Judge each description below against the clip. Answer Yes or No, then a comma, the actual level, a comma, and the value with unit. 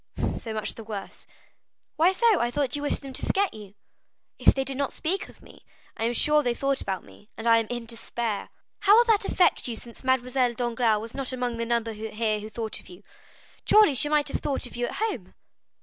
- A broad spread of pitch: No, average, 4.3 semitones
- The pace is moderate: No, fast, 230 wpm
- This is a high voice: Yes, high, 245 Hz